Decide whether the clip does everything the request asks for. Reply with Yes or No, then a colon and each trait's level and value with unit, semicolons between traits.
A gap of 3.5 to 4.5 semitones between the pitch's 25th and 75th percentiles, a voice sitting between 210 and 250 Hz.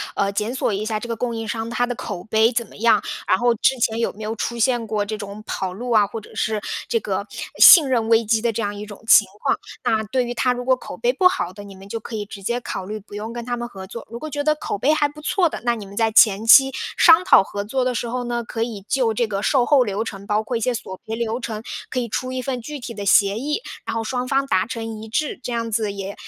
No: average, 2.8 semitones; high, 225 Hz